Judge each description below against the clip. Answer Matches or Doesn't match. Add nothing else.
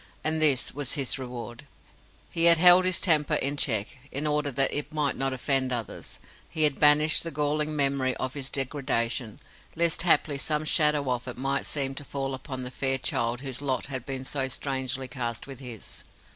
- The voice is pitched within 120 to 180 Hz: Matches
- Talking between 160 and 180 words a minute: Doesn't match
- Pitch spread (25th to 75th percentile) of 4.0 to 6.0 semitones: Doesn't match